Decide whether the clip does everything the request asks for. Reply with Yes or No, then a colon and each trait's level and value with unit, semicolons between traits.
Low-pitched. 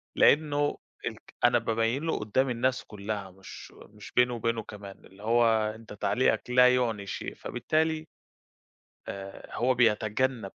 Yes: low, 115 Hz